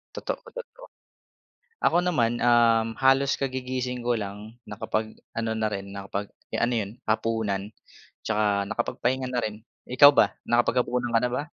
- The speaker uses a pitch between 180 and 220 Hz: No, low, 115 Hz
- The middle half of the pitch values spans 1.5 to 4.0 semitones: Yes, average, 2.7 semitones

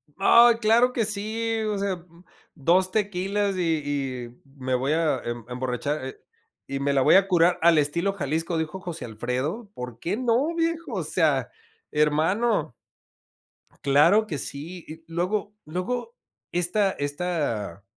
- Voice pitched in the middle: Yes, medium, 170 Hz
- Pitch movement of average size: No, wide, 6.2 semitones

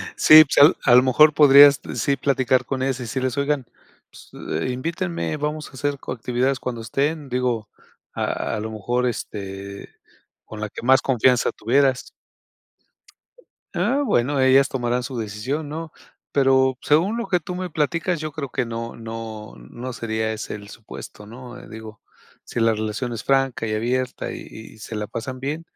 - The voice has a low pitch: Yes, low, 130 Hz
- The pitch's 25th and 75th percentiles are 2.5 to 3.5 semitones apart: No, average, 3.9 semitones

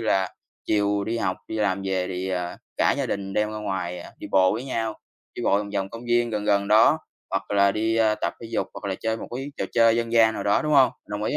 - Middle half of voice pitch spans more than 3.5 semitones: No, average, 2.8 semitones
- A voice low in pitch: Yes, low, 105 Hz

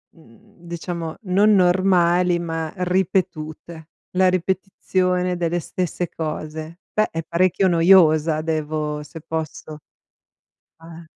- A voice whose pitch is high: No, medium, 170 Hz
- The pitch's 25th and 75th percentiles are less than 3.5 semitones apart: Yes, narrow, 2.4 semitones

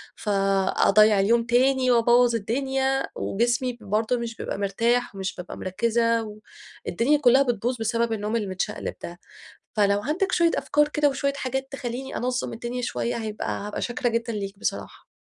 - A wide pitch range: No, average, 3.3 semitones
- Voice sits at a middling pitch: No, high, 235 Hz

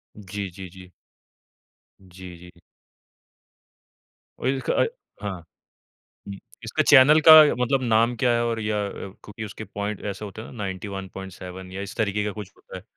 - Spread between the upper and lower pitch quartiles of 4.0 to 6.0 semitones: No, average, 3.3 semitones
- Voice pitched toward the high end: No, low, 100 Hz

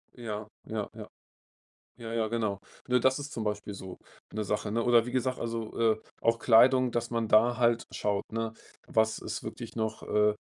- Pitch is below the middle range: Yes, low, 115 Hz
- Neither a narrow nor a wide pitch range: No, narrow, 1.7 semitones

